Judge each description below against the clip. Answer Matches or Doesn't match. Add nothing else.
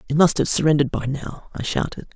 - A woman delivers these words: Doesn't match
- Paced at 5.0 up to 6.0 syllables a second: Doesn't match